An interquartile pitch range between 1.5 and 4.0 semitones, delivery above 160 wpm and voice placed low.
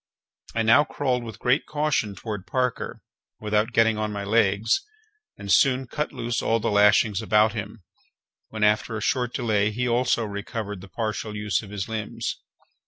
Yes: narrow, 2.4 semitones; average, 170 wpm; low, 110 Hz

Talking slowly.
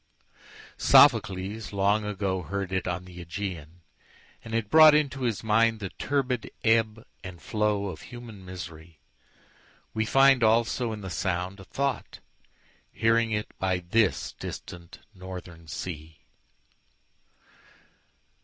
Yes: slow, 105 wpm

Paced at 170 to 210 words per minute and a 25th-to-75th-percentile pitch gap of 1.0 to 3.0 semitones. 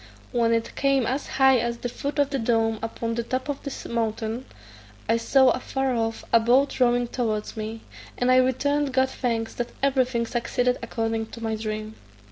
Yes: average, 185 wpm; narrow, 2.5 semitones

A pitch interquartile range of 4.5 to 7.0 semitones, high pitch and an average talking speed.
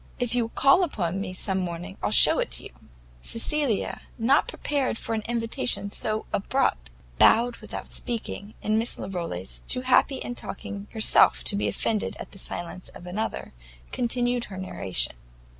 Yes: average, 4.8 semitones; high, 215 Hz; average, 160 wpm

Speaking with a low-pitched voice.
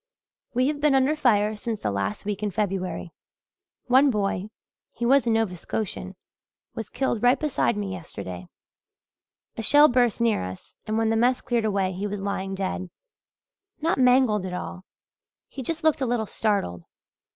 No: high, 215 Hz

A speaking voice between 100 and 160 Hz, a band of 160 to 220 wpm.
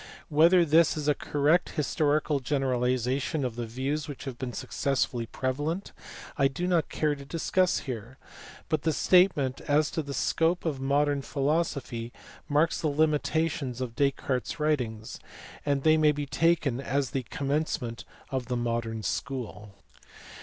No: medium, 140 Hz; average, 150 wpm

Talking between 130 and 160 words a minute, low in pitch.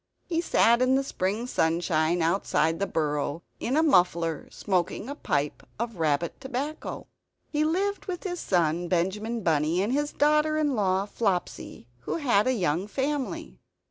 No: average, 155 wpm; high, 205 Hz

